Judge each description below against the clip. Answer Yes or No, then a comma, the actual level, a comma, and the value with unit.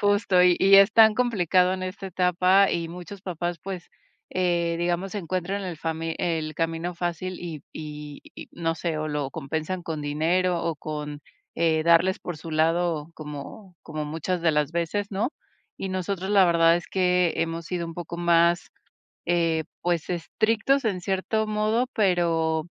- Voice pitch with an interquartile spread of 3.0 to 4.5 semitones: No, narrow, 2.4 semitones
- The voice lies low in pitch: No, medium, 175 Hz